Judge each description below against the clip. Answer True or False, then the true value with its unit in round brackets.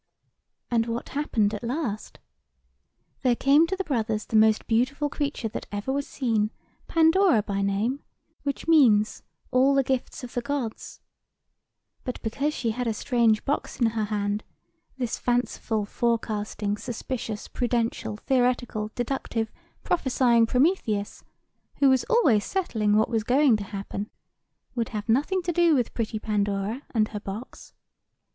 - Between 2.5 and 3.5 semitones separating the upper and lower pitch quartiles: False (4.0 semitones)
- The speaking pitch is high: True (235 Hz)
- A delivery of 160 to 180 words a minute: False (145 wpm)